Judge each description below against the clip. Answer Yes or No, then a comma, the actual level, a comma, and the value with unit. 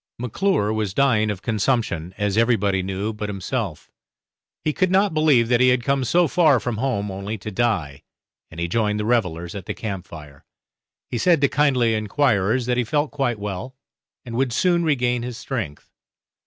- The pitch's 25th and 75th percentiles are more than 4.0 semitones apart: Yes, average, 4.7 semitones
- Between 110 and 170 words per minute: No, average, 180 wpm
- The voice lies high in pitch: No, low, 115 Hz